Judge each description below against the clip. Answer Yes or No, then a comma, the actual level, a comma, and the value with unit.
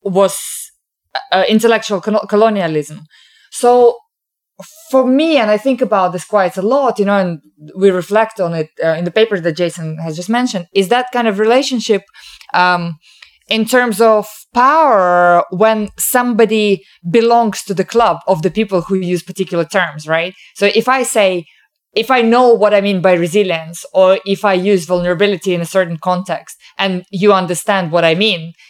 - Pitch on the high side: Yes, high, 195 Hz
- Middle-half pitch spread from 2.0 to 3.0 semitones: No, average, 4.0 semitones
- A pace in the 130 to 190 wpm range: Yes, average, 175 wpm